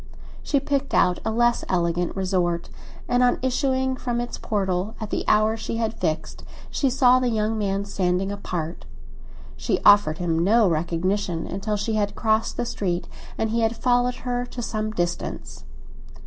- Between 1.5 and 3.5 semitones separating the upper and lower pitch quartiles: No, average, 4.8 semitones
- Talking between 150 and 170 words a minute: Yes, average, 165 wpm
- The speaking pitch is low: No, high, 215 Hz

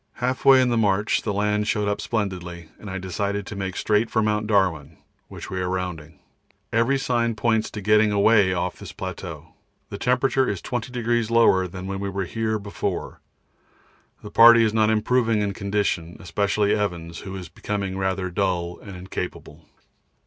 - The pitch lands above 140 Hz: No, low, 100 Hz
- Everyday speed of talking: Yes, average, 175 wpm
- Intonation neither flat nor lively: Yes, average, 3.0 semitones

